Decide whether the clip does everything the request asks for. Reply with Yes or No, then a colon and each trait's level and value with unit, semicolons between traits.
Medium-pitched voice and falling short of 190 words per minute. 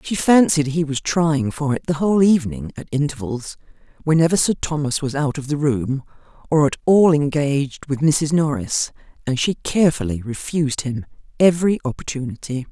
Yes: medium, 145 Hz; average, 160 wpm